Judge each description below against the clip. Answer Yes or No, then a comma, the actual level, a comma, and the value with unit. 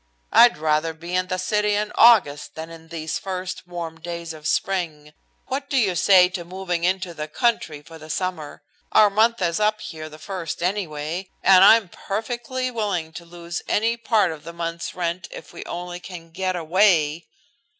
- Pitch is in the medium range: Yes, medium, 175 Hz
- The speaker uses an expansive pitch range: No, average, 3.7 semitones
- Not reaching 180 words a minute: No, average, 185 wpm